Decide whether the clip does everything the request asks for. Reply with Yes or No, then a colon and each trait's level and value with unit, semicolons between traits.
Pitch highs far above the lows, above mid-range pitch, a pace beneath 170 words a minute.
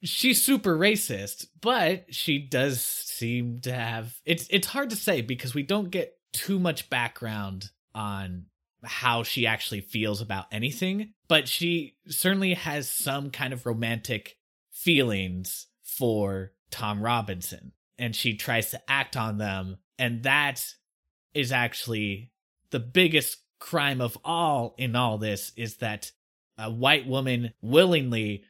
No: wide, 6.0 semitones; low, 125 Hz; slow, 135 wpm